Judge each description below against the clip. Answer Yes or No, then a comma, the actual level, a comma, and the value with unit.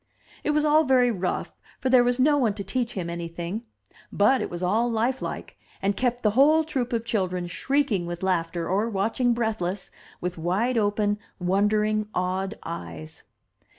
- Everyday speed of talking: Yes, average, 170 wpm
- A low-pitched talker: No, high, 210 Hz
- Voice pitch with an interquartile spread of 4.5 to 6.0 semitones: Yes, average, 5.2 semitones